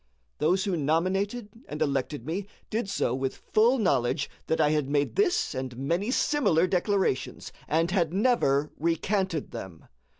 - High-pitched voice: No, medium, 165 Hz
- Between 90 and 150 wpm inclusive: Yes, average, 145 wpm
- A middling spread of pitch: No, wide, 5.8 semitones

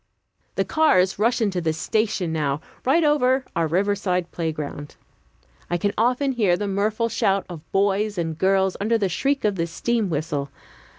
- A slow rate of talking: No, average, 165 wpm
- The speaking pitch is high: Yes, high, 195 Hz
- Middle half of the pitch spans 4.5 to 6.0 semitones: Yes, average, 5.0 semitones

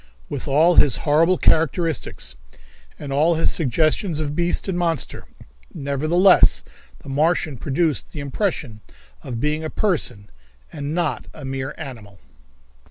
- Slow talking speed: Yes, slow, 130 wpm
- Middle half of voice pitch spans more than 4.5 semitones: No, average, 3.4 semitones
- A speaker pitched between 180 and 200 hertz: No, medium, 150 Hz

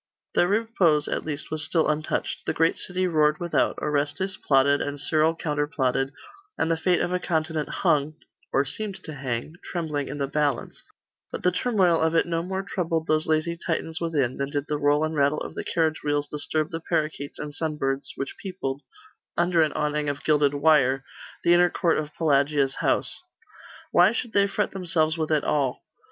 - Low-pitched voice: No, medium, 155 Hz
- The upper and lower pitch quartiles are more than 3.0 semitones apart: No, average, 2.7 semitones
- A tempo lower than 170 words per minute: No, average, 185 wpm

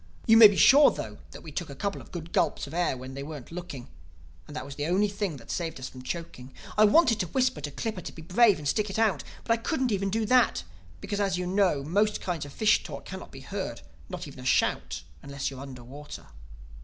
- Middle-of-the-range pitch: Yes, medium, 175 Hz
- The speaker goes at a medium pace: No, fast, 240 wpm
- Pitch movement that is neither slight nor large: No, wide, 6.9 semitones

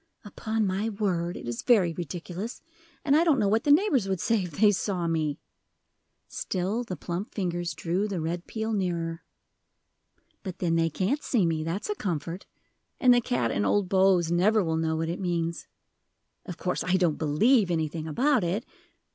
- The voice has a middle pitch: Yes, medium, 180 Hz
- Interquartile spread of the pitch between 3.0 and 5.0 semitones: Yes, average, 4.3 semitones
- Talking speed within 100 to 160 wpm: No, average, 180 wpm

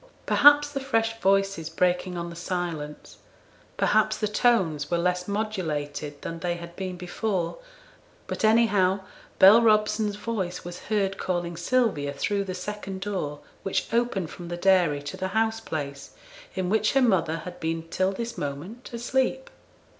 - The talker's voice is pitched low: No, high, 190 Hz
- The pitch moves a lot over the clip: No, average, 4.1 semitones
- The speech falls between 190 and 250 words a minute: No, average, 155 wpm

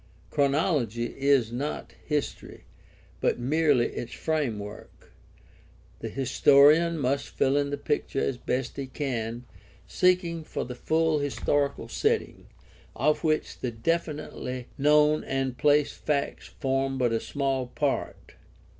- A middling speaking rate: No, slow, 120 wpm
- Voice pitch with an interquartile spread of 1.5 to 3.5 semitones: Yes, average, 3.1 semitones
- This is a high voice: No, medium, 140 Hz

